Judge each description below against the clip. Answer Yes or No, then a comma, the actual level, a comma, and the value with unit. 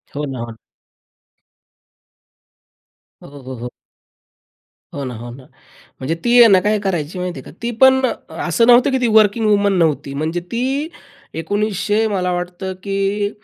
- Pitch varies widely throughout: Yes, wide, 5.9 semitones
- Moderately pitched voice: No, high, 195 Hz